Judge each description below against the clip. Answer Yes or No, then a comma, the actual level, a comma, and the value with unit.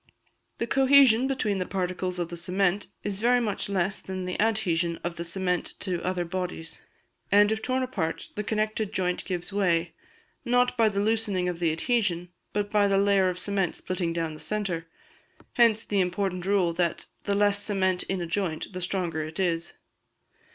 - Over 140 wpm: Yes, average, 180 wpm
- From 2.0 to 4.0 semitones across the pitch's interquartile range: Yes, average, 3.0 semitones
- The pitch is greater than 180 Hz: Yes, high, 190 Hz